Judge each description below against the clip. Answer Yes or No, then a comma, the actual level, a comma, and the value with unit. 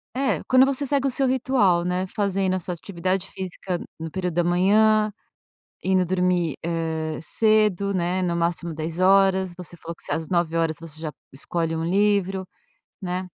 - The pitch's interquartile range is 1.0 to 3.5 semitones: Yes, average, 2.8 semitones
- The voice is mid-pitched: Yes, medium, 180 Hz